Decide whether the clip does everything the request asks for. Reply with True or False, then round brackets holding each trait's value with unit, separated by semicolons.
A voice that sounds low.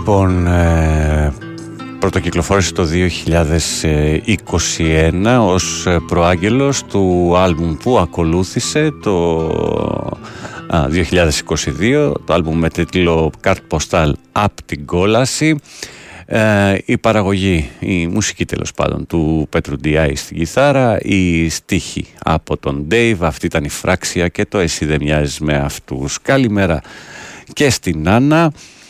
True (85 Hz)